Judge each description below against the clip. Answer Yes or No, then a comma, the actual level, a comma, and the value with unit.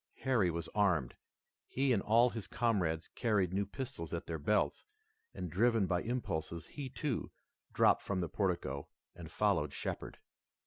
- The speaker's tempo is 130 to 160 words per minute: Yes, average, 150 wpm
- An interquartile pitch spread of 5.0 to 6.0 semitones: Yes, wide, 5.6 semitones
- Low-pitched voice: Yes, low, 100 Hz